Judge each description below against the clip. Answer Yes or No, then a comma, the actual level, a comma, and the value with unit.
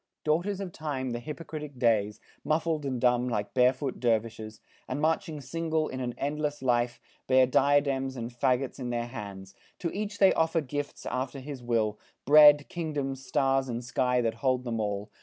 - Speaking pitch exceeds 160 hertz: No, low, 130 Hz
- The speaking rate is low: No, average, 170 wpm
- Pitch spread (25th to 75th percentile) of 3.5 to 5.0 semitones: Yes, average, 3.8 semitones